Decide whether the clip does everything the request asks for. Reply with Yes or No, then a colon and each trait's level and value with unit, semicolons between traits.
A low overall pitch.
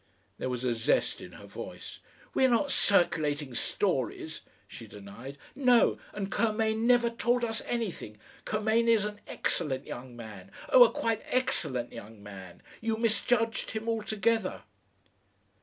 No: high, 215 Hz